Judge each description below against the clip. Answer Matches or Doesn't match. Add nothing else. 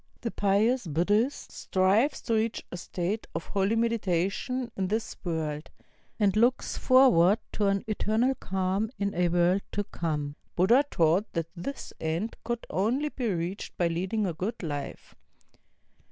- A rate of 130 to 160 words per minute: Matches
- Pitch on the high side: Matches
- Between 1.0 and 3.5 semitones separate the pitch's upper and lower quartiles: Doesn't match